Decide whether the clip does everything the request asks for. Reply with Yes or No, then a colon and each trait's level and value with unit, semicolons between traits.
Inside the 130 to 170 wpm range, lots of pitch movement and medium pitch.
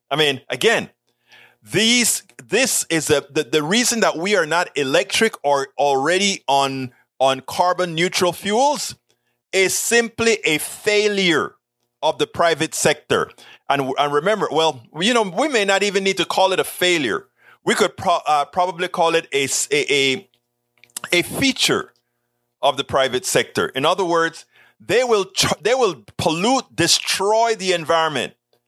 Yes: average, 155 wpm; wide, 6.7 semitones; medium, 165 Hz